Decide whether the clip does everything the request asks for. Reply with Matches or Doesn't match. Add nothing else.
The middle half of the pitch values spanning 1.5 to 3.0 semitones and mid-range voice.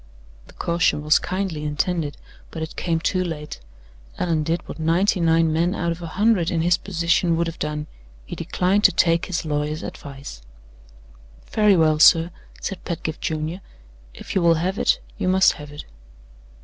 Matches